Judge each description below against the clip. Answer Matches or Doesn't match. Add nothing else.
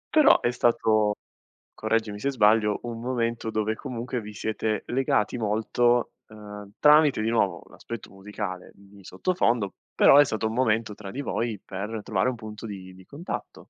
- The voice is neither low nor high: Doesn't match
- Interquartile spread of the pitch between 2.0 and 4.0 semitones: Matches